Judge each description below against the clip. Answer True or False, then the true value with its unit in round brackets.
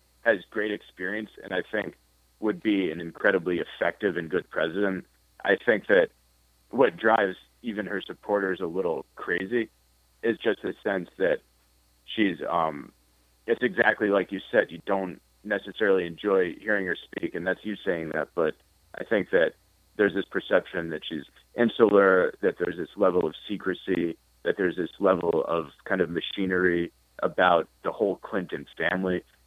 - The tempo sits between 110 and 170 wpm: True (160 wpm)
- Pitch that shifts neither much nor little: False (8.1 semitones)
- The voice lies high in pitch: False (85 Hz)